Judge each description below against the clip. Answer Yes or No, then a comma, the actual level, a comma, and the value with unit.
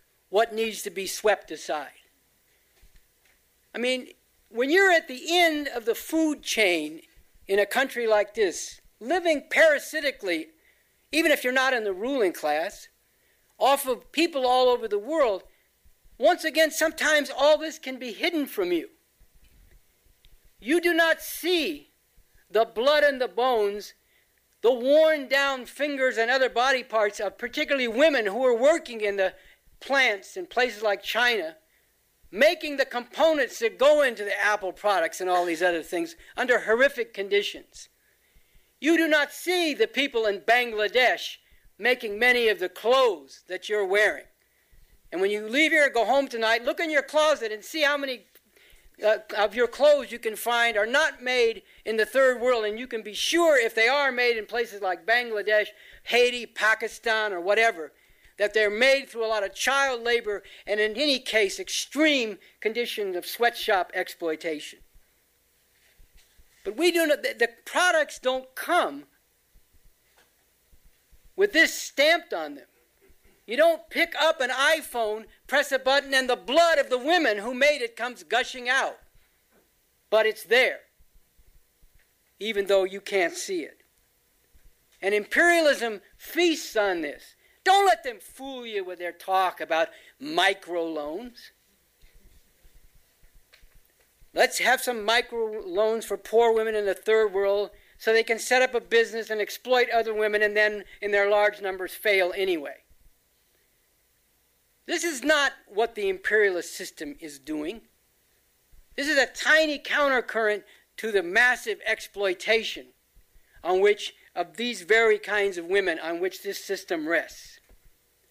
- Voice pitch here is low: No, high, 245 Hz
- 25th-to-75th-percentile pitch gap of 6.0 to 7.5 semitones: Yes, wide, 6.4 semitones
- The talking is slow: No, average, 150 wpm